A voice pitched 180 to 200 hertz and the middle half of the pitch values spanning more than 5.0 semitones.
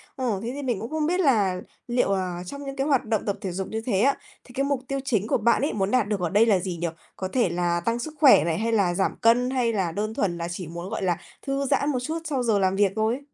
No: high, 220 Hz; wide, 5.6 semitones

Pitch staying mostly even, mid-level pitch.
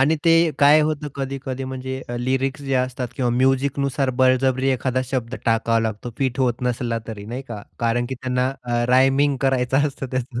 No: narrow, 1.7 semitones; low, 130 Hz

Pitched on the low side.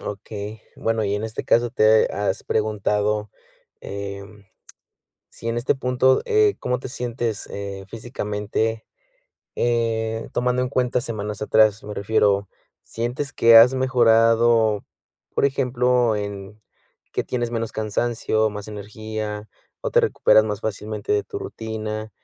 Yes: low, 110 Hz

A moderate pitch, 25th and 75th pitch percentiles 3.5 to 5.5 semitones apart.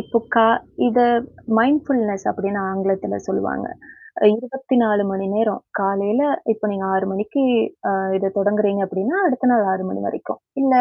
No: high, 210 Hz; average, 4.0 semitones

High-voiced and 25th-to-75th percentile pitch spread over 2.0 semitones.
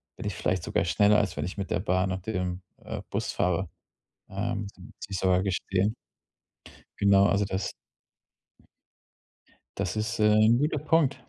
No: low, 100 Hz; narrow, 2.5 semitones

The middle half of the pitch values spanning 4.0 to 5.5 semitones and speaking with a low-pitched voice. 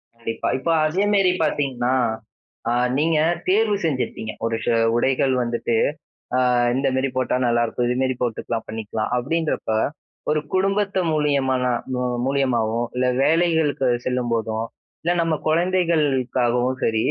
Yes: average, 4.9 semitones; low, 130 Hz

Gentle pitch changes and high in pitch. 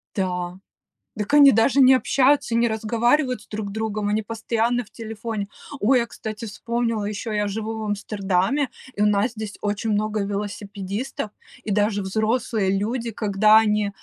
Yes: narrow, 2.1 semitones; high, 215 Hz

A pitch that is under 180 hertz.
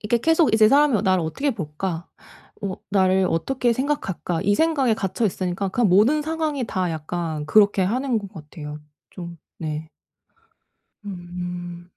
No: high, 190 Hz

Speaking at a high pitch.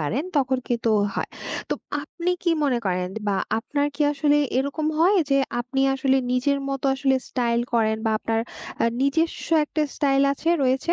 Yes: very high, 270 Hz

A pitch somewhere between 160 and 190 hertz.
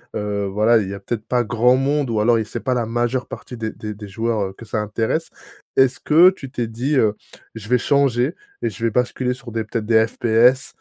No: low, 115 Hz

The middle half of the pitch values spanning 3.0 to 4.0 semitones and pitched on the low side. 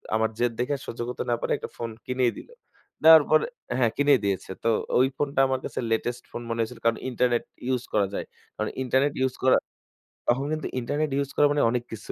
Yes: average, 3.4 semitones; low, 125 Hz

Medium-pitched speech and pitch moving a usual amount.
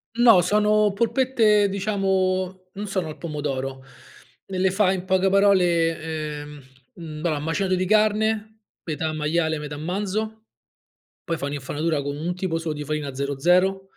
Yes: medium, 180 Hz; average, 4.6 semitones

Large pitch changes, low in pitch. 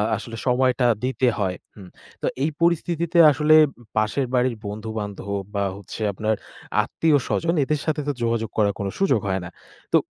Yes: wide, 6.2 semitones; low, 120 Hz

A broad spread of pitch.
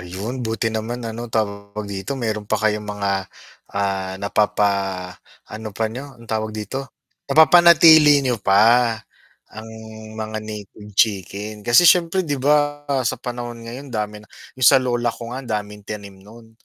No: average, 3.1 semitones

